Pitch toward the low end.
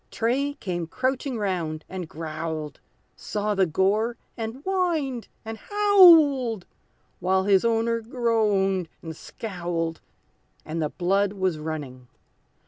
No: high, 200 Hz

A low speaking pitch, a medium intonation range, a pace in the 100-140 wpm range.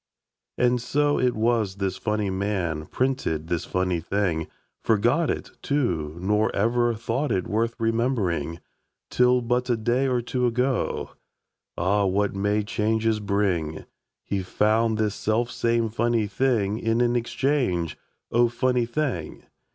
Yes: low, 110 Hz; average, 3.7 semitones; slow, 135 wpm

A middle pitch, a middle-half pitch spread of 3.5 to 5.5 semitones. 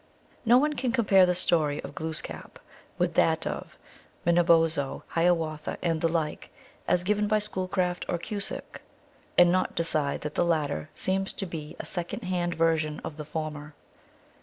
No: medium, 170 Hz; average, 3.0 semitones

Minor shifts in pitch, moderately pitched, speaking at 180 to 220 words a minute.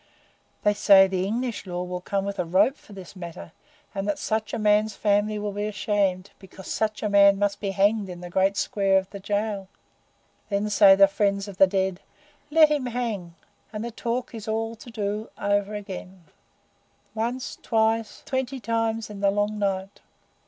No: narrow, 2.1 semitones; high, 205 Hz; average, 185 wpm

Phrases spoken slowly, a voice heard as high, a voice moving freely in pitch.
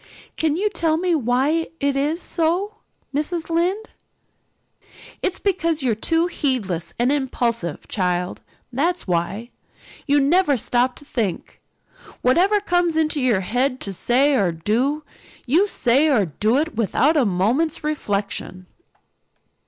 Yes: slow, 130 wpm; very high, 280 Hz; wide, 6.3 semitones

